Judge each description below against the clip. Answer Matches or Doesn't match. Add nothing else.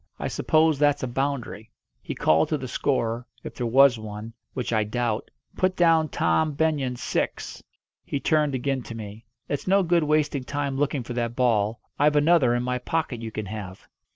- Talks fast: Doesn't match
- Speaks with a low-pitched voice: Matches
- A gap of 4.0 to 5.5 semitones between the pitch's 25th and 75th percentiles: Matches